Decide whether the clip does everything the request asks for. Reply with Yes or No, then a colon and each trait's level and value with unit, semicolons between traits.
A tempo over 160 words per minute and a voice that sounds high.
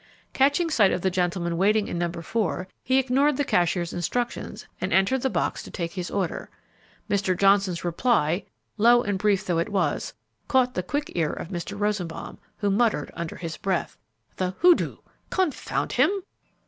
Yes: average, 170 wpm; high, 195 Hz